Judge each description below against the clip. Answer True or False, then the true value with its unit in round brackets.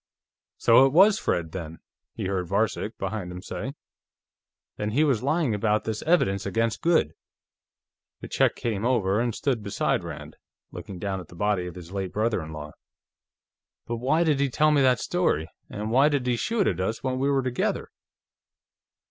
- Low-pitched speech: True (110 Hz)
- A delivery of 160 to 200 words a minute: True (180 wpm)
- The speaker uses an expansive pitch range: True (5.9 semitones)